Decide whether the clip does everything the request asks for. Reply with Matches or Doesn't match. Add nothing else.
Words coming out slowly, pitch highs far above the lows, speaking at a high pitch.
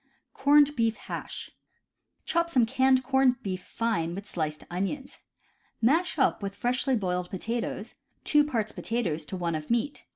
Doesn't match